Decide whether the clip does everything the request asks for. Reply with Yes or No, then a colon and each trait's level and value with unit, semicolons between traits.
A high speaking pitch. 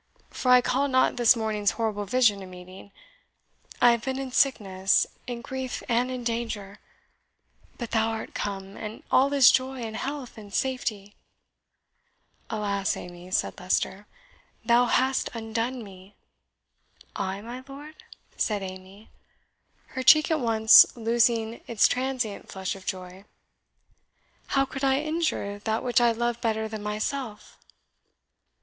Yes: high, 230 Hz